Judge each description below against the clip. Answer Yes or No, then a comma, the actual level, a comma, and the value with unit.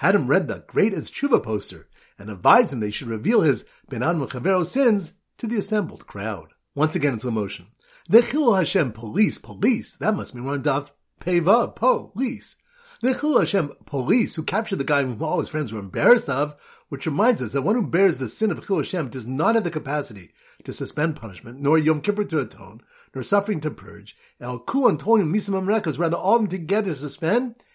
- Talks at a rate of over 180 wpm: Yes, average, 200 wpm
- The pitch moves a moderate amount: No, wide, 8.2 semitones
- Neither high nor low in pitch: Yes, medium, 160 Hz